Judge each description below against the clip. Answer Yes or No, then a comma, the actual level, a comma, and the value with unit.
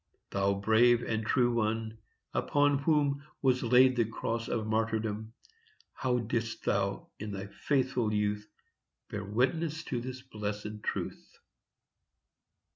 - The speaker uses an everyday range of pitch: Yes, average, 3.2 semitones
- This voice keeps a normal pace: No, slow, 120 wpm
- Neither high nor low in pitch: No, low, 115 Hz